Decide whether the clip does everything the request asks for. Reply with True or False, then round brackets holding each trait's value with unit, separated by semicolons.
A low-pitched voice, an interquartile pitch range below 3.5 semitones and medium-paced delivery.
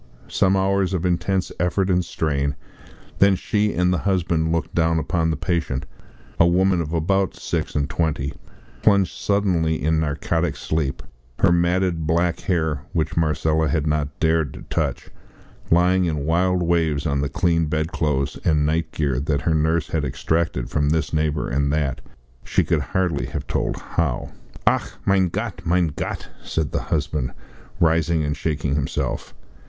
True (80 Hz; 2.8 semitones; 160 wpm)